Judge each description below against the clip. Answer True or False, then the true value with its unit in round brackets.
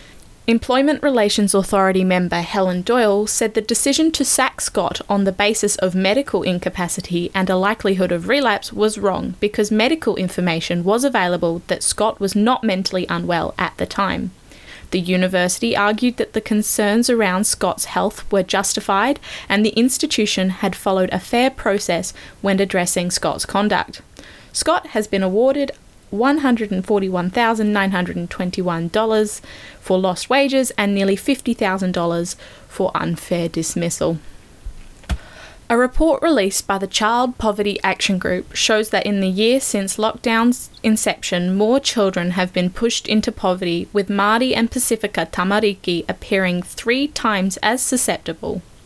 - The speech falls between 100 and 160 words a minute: True (135 wpm)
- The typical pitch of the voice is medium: False (205 Hz)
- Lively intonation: False (3.6 semitones)